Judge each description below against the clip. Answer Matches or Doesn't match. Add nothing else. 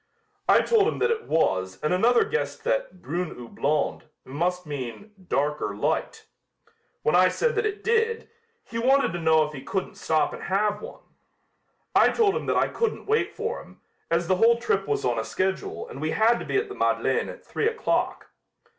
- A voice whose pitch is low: Doesn't match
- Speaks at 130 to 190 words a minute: Doesn't match